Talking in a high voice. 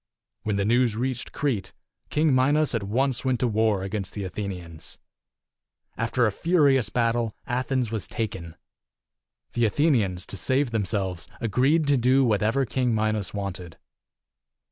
No: low, 115 Hz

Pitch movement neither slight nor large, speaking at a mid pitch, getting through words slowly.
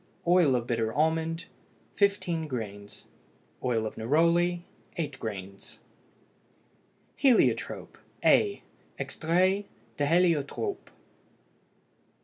No: wide, 6.8 semitones; medium, 160 Hz; slow, 80 wpm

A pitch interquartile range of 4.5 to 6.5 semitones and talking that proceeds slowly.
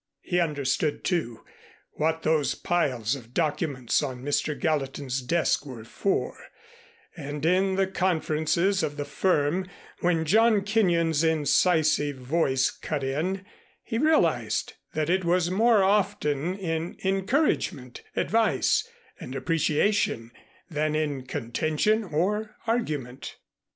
Yes: average, 4.8 semitones; slow, 115 wpm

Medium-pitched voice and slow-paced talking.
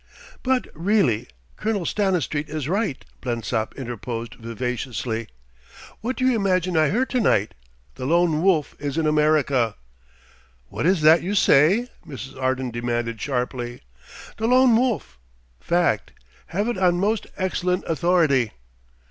Yes: medium, 155 Hz; slow, 130 wpm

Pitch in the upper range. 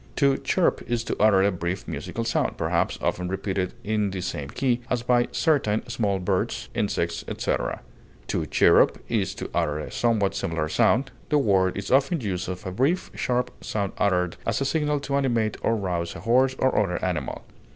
No: low, 105 Hz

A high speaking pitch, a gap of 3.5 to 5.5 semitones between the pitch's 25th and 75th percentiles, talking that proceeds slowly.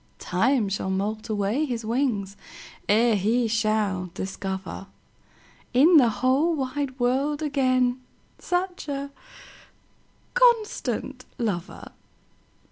Yes: high, 245 Hz; average, 5.1 semitones; slow, 80 wpm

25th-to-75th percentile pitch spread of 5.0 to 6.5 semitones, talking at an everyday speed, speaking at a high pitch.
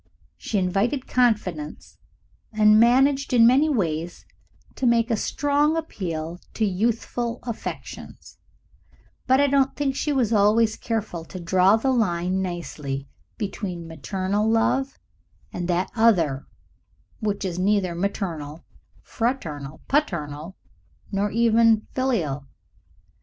No: wide, 5.5 semitones; slow, 115 wpm; high, 210 Hz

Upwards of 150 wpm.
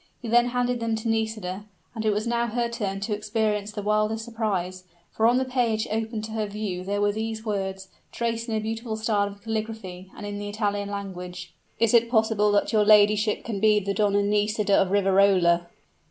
Yes: average, 195 wpm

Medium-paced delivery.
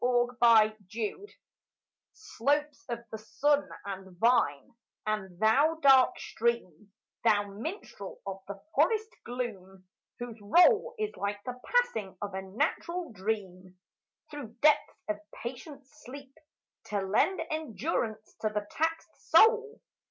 No: slow, 120 wpm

